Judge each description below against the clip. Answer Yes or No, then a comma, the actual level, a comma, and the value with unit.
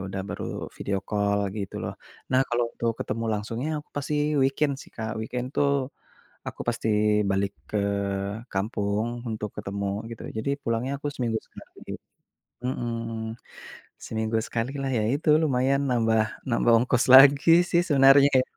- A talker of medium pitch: No, low, 115 Hz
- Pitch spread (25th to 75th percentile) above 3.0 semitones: Yes, average, 3.6 semitones